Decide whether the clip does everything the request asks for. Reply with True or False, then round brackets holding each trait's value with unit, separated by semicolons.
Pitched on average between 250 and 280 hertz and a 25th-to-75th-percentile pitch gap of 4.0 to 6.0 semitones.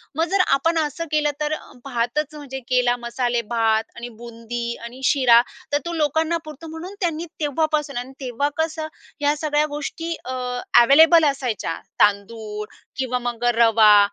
True (270 Hz; 4.5 semitones)